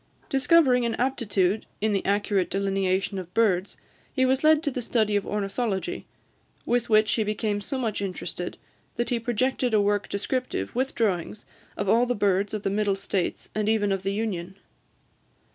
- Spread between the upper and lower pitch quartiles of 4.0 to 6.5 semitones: No, average, 3.6 semitones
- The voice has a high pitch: Yes, high, 210 Hz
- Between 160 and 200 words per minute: Yes, average, 175 wpm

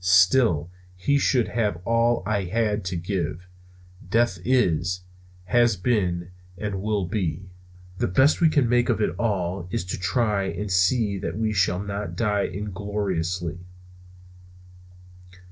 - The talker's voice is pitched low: Yes, low, 100 Hz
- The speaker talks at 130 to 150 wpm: Yes, slow, 135 wpm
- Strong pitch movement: No, average, 4.0 semitones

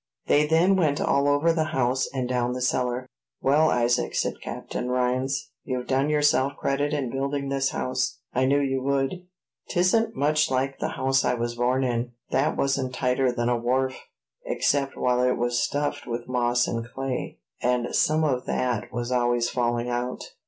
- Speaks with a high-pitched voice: No, low, 130 Hz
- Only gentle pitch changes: Yes, narrow, 2.3 semitones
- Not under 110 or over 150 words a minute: No, average, 175 wpm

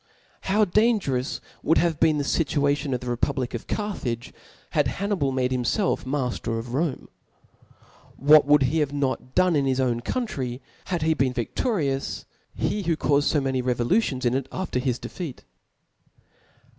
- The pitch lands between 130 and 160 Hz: Yes, medium, 140 Hz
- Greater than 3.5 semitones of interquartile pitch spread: Yes, average, 4.3 semitones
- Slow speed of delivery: No, average, 165 wpm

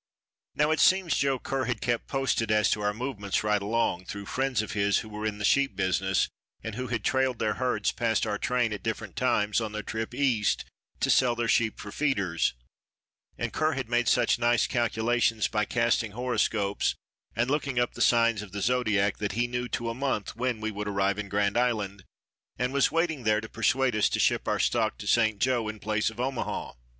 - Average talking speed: No, fast, 210 wpm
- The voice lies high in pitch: No, low, 115 Hz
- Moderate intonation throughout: Yes, average, 3.1 semitones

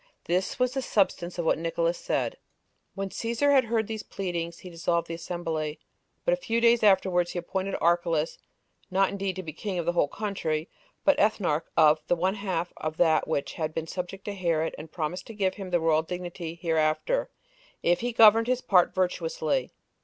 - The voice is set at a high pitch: No, medium, 180 Hz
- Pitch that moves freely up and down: No, average, 3.7 semitones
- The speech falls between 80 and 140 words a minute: No, average, 195 wpm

